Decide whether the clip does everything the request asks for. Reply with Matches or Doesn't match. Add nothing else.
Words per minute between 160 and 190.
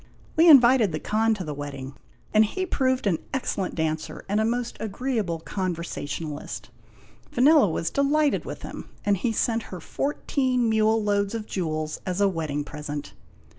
Matches